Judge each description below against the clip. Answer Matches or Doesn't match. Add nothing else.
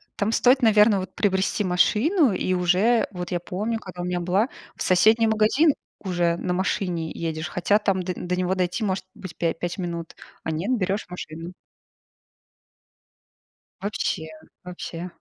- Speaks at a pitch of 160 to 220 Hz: Matches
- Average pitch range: Matches